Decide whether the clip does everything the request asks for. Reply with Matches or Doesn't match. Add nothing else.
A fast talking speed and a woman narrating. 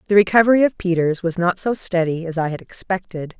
Matches